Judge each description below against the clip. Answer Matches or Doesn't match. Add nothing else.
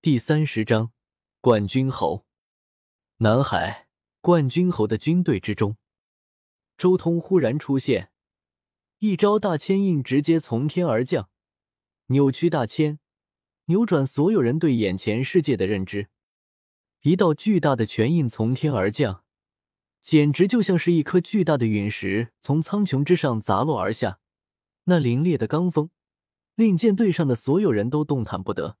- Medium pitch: Matches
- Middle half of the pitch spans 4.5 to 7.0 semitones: Doesn't match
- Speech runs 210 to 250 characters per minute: Matches